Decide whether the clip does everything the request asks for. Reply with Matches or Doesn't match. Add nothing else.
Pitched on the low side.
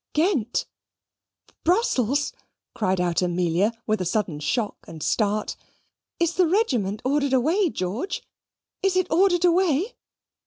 Doesn't match